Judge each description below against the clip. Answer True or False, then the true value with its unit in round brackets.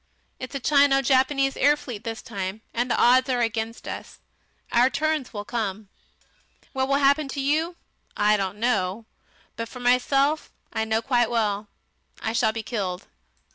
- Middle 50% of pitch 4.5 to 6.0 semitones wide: False (3.7 semitones)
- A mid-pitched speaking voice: False (240 Hz)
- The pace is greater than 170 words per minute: False (165 wpm)